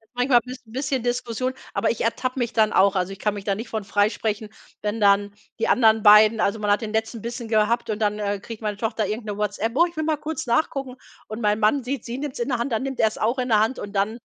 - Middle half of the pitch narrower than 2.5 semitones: No, average, 2.9 semitones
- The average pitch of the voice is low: No, high, 225 Hz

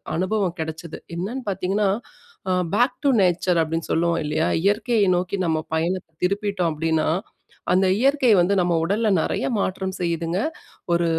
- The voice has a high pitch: No, medium, 180 Hz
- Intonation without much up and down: No, average, 3.3 semitones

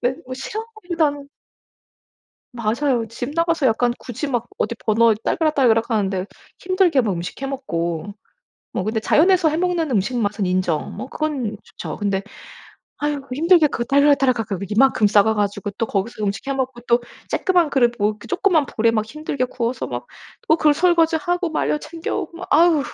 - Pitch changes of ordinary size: No, wide, 6.2 semitones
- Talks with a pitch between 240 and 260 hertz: Yes, very high, 255 Hz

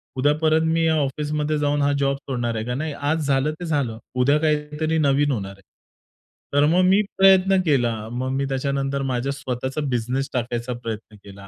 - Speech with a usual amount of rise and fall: Yes, average, 3.4 semitones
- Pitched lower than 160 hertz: Yes, medium, 140 Hz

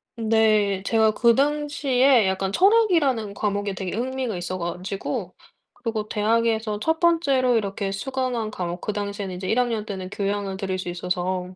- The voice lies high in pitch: Yes, high, 215 Hz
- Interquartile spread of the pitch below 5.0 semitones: Yes, average, 4.4 semitones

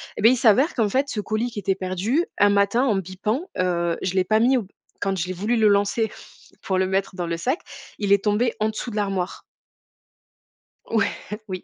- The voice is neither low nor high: No, high, 205 Hz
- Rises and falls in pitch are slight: No, average, 3.3 semitones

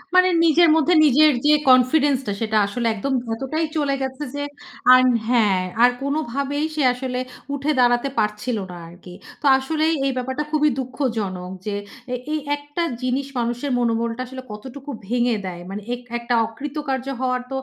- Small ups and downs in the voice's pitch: No, average, 3.6 semitones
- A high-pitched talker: Yes, very high, 260 Hz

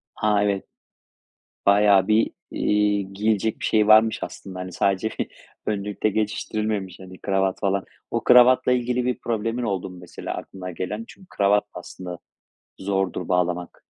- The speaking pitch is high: No, low, 100 Hz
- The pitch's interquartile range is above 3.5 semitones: No, narrow, 2.4 semitones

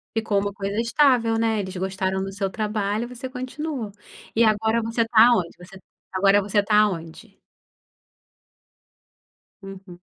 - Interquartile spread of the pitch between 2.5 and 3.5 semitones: Yes, average, 2.9 semitones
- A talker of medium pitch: No, high, 210 Hz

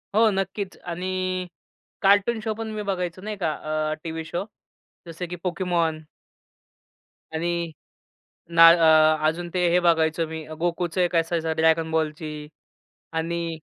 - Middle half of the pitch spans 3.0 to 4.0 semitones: No, narrow, 2.4 semitones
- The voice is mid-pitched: Yes, medium, 170 Hz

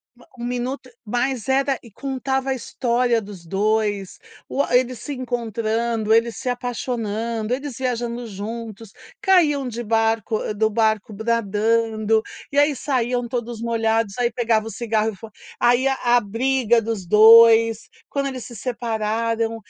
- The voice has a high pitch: Yes, high, 230 Hz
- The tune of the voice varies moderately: No, narrow, 2.1 semitones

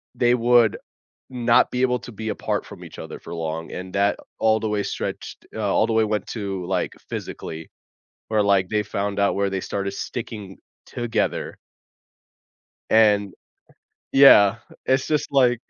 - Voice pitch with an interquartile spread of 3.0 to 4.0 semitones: Yes, average, 3.3 semitones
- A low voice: Yes, low, 105 Hz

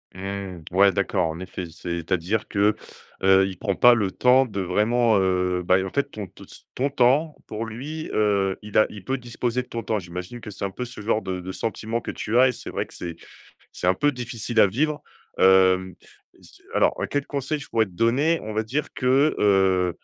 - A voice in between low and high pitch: No, low, 105 Hz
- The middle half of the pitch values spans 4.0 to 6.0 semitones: Yes, average, 4.7 semitones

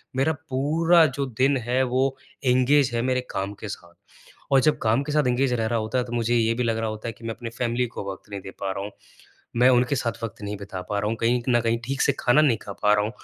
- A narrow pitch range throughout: No, average, 3.1 semitones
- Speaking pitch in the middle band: No, low, 120 Hz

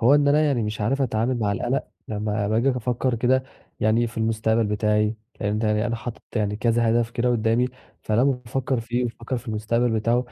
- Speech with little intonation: Yes, narrow, 2.3 semitones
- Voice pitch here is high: No, low, 115 Hz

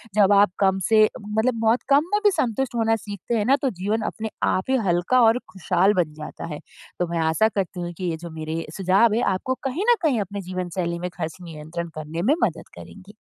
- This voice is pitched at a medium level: No, high, 200 Hz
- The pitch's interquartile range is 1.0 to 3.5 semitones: No, average, 4.6 semitones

